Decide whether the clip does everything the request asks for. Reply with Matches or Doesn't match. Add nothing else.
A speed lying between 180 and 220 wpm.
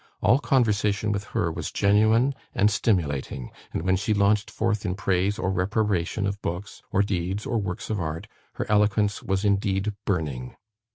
Doesn't match